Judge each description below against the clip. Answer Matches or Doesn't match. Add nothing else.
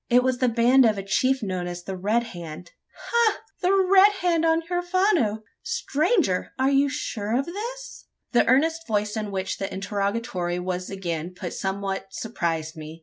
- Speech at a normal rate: Matches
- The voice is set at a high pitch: Matches